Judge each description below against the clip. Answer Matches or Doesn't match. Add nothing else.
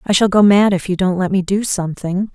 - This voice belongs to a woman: Matches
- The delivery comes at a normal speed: Doesn't match